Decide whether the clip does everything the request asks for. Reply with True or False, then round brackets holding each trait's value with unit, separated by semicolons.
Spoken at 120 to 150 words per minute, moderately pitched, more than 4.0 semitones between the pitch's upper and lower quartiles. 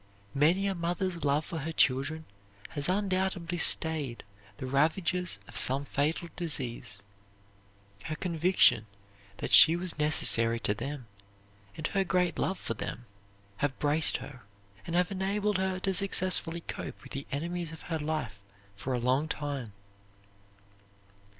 True (140 wpm; 160 Hz; 4.7 semitones)